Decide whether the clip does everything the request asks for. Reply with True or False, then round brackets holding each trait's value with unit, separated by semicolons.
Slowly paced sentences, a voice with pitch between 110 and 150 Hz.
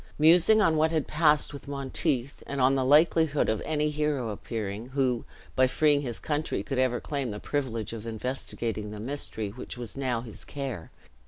False (180 wpm; 135 Hz)